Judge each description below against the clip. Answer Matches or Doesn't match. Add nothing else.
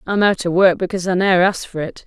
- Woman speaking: Matches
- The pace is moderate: Doesn't match